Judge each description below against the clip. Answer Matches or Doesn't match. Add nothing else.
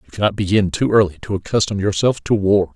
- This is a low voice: Matches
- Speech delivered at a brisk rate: Matches